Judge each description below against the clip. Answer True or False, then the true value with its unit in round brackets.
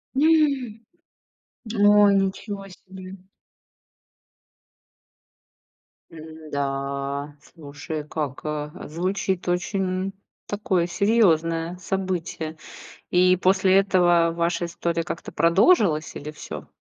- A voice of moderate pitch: True (175 Hz)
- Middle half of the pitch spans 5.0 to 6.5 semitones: False (3.6 semitones)